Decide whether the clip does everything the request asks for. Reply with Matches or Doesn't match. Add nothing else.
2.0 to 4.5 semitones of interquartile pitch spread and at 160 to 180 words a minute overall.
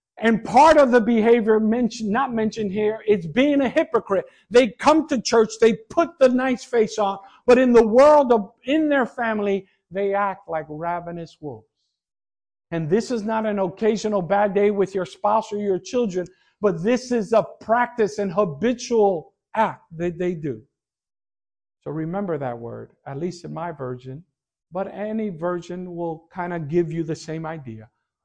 Doesn't match